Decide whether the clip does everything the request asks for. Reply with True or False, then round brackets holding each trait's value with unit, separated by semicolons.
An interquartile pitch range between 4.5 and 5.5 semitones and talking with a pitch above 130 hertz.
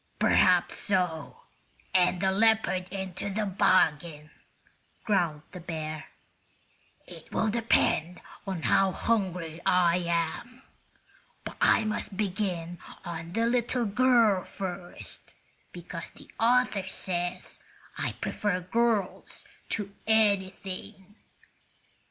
False (3.6 semitones; 190 Hz)